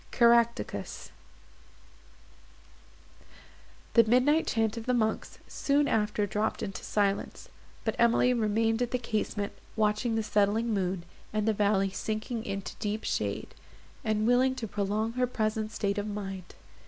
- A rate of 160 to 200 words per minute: No, slow, 135 wpm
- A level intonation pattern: Yes, narrow, 2.2 semitones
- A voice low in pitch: No, high, 220 Hz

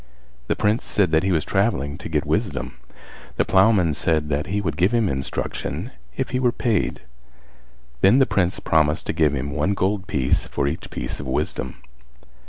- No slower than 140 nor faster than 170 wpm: No, average, 185 wpm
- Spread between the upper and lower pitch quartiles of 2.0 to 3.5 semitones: No, wide, 5.5 semitones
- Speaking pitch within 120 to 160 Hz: No, very low, 85 Hz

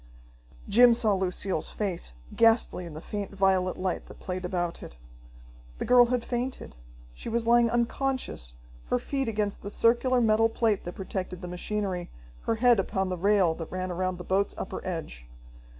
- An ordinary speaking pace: Yes, average, 170 wpm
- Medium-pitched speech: No, high, 195 Hz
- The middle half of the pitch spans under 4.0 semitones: No, average, 4.3 semitones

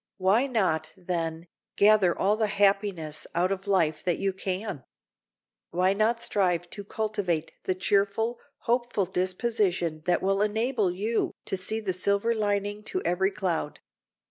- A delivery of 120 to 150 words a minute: Yes, average, 145 wpm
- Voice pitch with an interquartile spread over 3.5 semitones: No, average, 2.9 semitones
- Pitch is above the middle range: Yes, high, 195 Hz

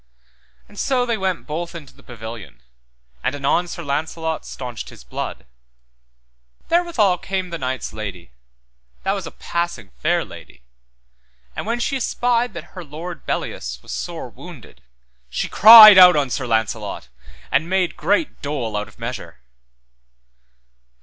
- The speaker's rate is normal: Yes, average, 145 wpm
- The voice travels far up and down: Yes, wide, 8.3 semitones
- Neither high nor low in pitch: Yes, medium, 160 Hz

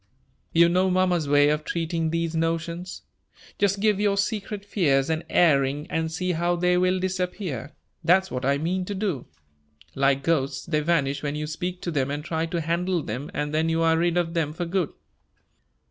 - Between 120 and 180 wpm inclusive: No, average, 190 wpm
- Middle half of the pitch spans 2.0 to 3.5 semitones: Yes, average, 3.2 semitones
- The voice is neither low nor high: Yes, medium, 165 Hz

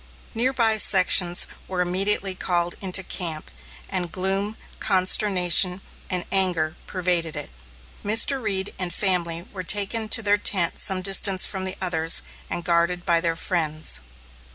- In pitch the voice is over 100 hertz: Yes, medium, 185 Hz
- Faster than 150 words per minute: No, average, 140 wpm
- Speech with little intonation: Yes, narrow, 2.3 semitones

